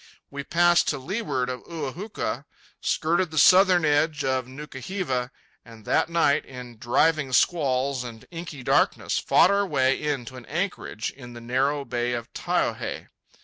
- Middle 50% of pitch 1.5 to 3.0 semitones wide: No, average, 4.8 semitones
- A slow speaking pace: No, average, 160 wpm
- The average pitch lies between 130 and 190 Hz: Yes, medium, 140 Hz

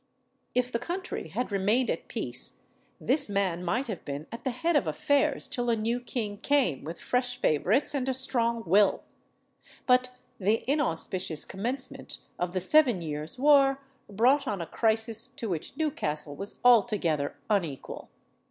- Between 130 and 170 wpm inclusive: Yes, average, 155 wpm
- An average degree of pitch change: No, wide, 6.0 semitones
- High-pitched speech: Yes, high, 225 Hz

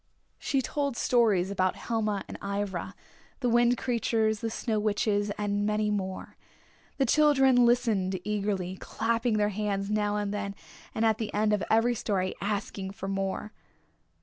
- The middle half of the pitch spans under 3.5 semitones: Yes, narrow, 2.4 semitones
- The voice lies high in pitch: Yes, high, 210 Hz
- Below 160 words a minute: Yes, average, 150 wpm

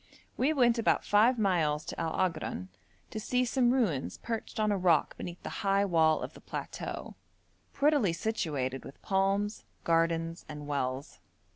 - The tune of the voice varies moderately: No, wide, 5.9 semitones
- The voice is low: No, medium, 185 Hz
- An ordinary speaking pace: Yes, average, 155 wpm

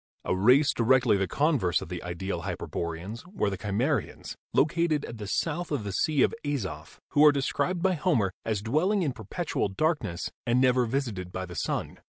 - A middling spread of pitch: No, wide, 7.5 semitones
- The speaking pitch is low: Yes, low, 120 Hz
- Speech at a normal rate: Yes, average, 185 wpm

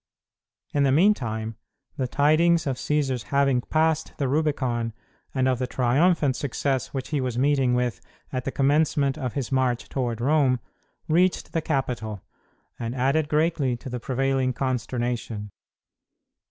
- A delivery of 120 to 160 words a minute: Yes, average, 140 wpm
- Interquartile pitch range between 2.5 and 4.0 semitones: Yes, average, 3.0 semitones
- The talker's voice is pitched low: Yes, low, 130 Hz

